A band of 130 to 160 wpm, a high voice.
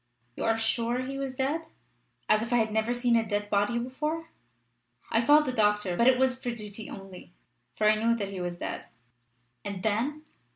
No: average, 200 wpm; high, 230 Hz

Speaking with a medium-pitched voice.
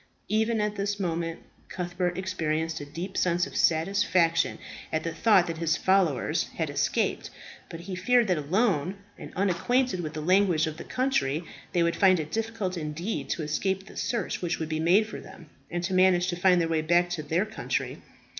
Yes: medium, 175 Hz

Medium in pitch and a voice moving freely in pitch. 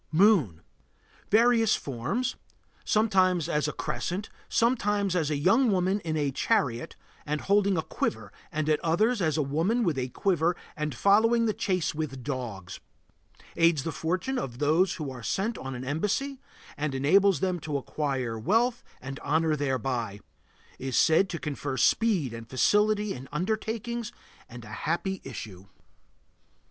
Yes: medium, 160 Hz; wide, 7.1 semitones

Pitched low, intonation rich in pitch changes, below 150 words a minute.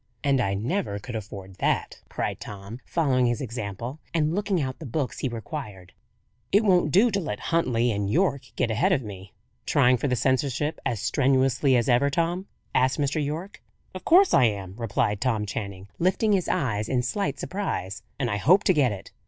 No: low, 130 Hz; wide, 6.9 semitones; average, 190 wpm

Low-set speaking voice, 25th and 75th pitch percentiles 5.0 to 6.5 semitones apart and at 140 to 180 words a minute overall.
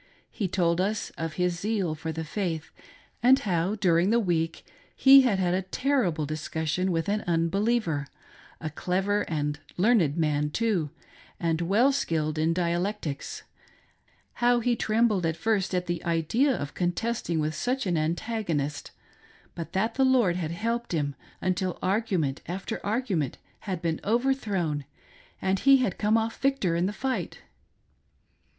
No: medium, 180 Hz; average, 5.3 semitones; average, 155 wpm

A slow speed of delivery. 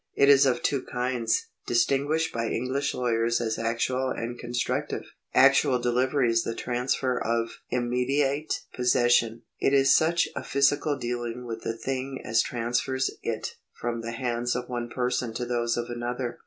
No: average, 165 wpm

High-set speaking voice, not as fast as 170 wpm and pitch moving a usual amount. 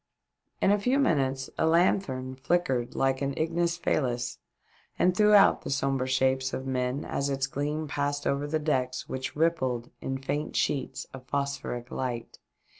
No: low, 135 Hz; average, 160 wpm; average, 3.2 semitones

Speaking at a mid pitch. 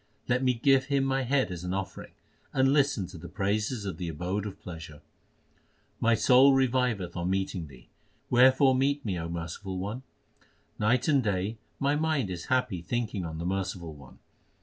No: low, 105 Hz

